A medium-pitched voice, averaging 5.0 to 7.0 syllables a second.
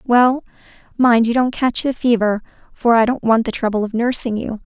No: high, 235 Hz; 5.1 syllables/s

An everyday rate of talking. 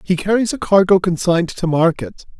Yes: average, 175 wpm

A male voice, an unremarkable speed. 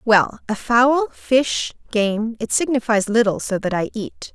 No: female; average, 150 wpm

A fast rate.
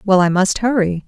Yes: fast, 225 wpm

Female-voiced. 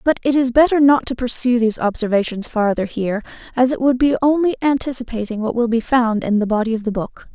Yes: female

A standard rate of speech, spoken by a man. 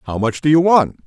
No: fast, 280 wpm; male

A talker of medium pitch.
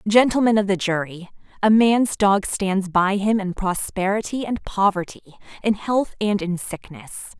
No: high, 200 Hz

